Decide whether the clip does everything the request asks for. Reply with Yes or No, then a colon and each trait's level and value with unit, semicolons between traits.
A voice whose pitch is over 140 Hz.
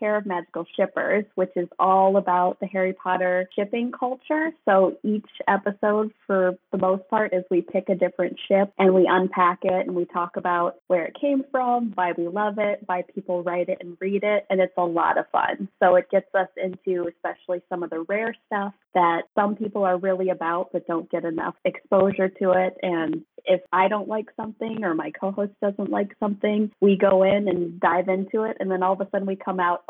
Yes: high, 190 Hz